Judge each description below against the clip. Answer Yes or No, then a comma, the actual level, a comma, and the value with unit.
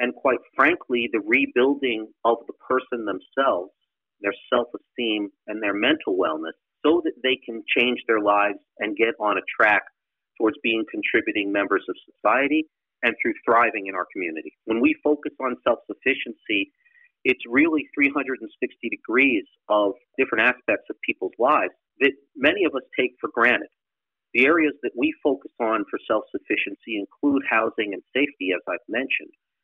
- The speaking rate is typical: Yes, average, 160 wpm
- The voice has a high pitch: No, low, 135 Hz